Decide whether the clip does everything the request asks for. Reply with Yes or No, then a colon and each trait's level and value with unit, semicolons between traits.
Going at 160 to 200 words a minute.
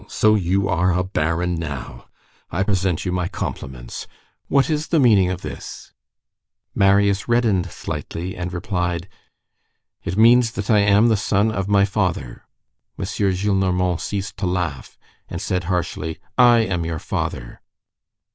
No: average, 145 wpm